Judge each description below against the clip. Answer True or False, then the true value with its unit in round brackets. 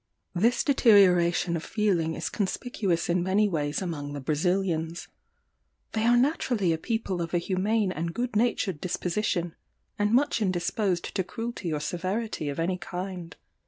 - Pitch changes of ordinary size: True (4.1 semitones)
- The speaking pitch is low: False (185 Hz)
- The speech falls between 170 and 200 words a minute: False (150 wpm)